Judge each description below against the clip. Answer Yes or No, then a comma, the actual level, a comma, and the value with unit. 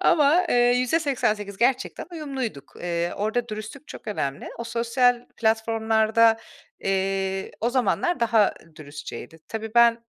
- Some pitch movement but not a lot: Yes, average, 3.3 semitones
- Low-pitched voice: No, high, 225 Hz